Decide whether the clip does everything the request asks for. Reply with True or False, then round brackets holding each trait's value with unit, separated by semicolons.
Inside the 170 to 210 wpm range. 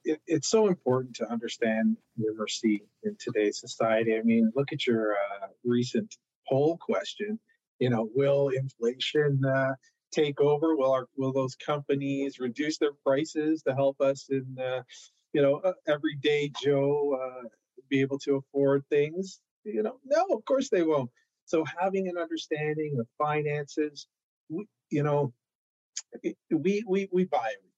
False (155 wpm)